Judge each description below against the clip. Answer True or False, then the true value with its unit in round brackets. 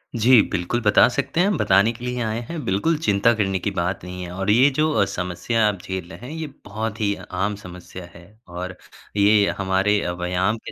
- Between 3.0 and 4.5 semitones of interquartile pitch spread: True (4.0 semitones)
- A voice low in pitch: True (100 Hz)